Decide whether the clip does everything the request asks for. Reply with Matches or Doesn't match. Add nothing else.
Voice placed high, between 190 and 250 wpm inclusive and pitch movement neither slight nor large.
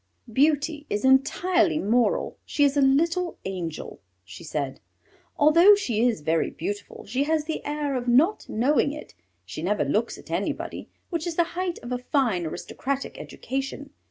Doesn't match